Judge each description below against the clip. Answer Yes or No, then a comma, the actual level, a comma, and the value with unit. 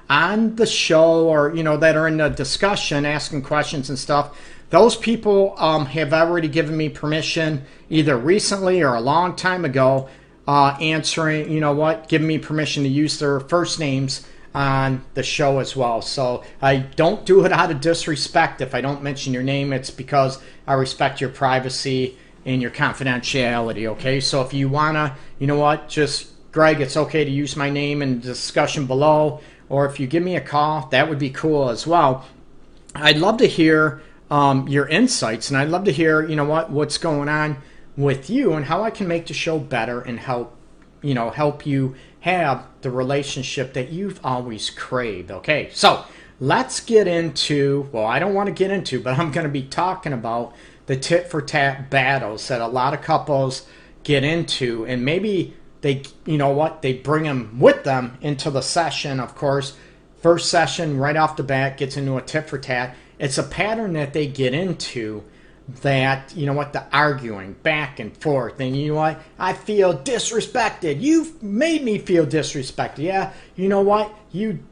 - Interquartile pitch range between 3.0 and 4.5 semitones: Yes, average, 3.3 semitones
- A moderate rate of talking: Yes, average, 190 wpm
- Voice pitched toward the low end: No, medium, 145 Hz